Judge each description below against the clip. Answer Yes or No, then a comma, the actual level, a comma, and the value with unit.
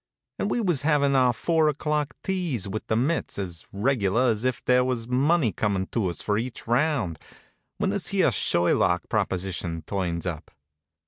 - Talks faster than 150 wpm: Yes, average, 170 wpm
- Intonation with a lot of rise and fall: Yes, wide, 6.9 semitones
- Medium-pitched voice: No, low, 120 Hz